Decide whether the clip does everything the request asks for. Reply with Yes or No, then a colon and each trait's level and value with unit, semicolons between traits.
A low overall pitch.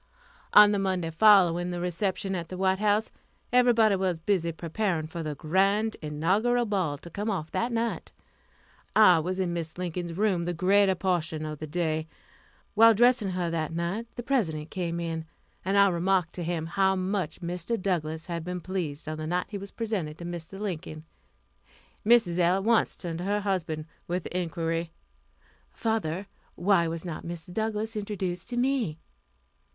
No: medium, 180 Hz